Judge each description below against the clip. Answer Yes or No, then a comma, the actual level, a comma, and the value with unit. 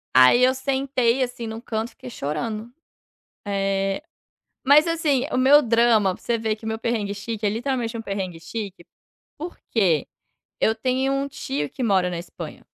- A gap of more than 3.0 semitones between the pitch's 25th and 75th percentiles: Yes, average, 4.5 semitones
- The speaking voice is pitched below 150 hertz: No, high, 225 Hz